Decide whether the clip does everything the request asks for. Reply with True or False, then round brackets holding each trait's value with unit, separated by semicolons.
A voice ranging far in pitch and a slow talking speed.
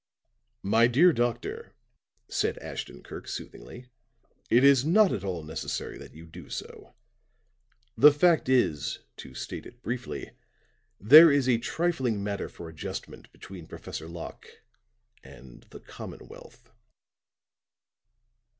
True (8.5 semitones; 120 wpm)